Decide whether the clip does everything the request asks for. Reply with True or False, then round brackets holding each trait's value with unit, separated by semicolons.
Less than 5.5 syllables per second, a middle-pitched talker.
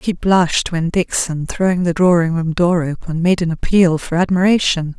True (4.9 syllables/s; 175 Hz)